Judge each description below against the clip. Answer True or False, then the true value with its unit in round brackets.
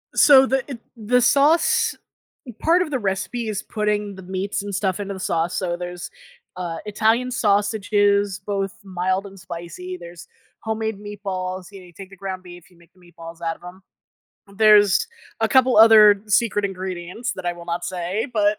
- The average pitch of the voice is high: True (195 Hz)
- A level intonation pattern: False (3.0 semitones)